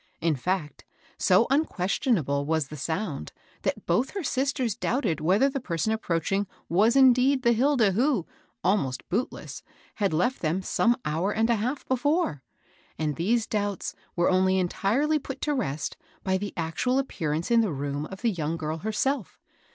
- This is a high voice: Yes, high, 200 Hz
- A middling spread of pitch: No, wide, 7.3 semitones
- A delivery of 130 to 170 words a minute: Yes, average, 160 wpm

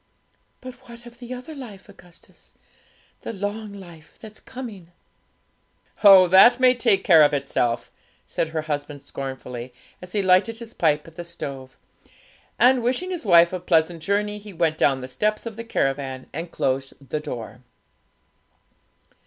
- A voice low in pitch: No, medium, 180 Hz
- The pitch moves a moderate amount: No, wide, 7.1 semitones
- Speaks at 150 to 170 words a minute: Yes, average, 155 wpm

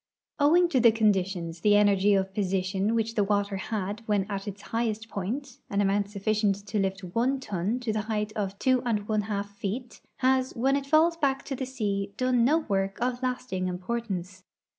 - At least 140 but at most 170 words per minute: No, average, 190 wpm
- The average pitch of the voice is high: Yes, high, 210 Hz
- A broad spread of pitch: No, average, 4.0 semitones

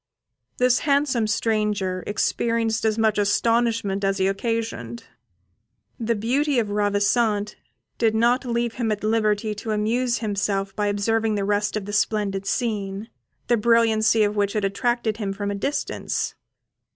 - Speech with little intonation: Yes, narrow, 2.2 semitones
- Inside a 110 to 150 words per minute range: Yes, average, 145 wpm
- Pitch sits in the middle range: No, high, 215 Hz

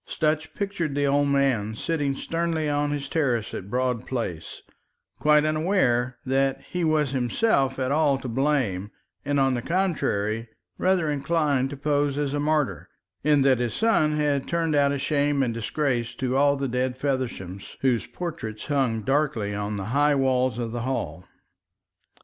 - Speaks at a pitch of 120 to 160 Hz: Yes, medium, 140 Hz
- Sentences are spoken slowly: No, average, 165 wpm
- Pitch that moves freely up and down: No, average, 3.5 semitones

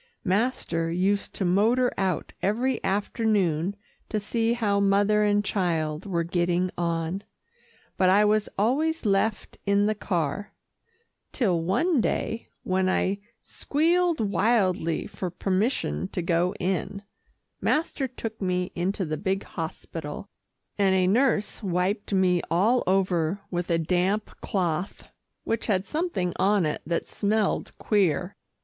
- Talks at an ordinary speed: No, slow, 130 wpm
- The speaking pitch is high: Yes, high, 195 Hz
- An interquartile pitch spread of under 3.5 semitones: Yes, average, 3.1 semitones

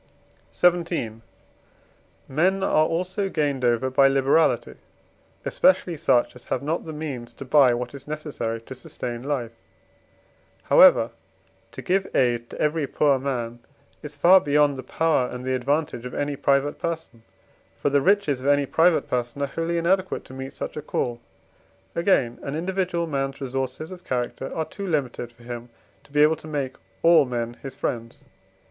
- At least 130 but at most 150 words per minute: No, average, 165 wpm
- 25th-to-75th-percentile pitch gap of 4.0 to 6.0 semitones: Yes, average, 4.3 semitones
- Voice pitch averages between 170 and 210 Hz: No, medium, 140 Hz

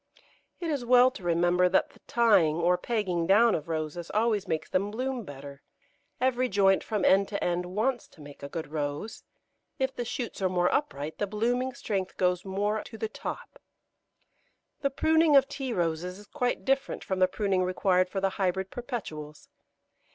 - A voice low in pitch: No, high, 195 Hz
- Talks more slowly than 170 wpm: No, average, 180 wpm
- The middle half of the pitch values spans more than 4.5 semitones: Yes, wide, 5.4 semitones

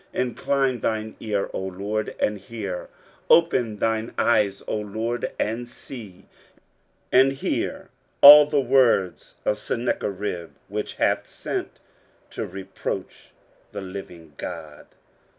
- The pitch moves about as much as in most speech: Yes, average, 3.8 semitones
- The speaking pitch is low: Yes, low, 110 Hz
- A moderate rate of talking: No, slow, 115 wpm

